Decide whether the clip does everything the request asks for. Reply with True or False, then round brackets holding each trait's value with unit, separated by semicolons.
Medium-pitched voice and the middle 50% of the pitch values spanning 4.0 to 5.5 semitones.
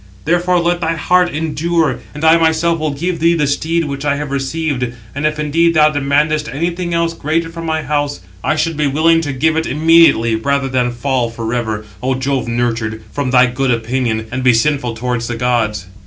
True (145 Hz; 4.6 semitones)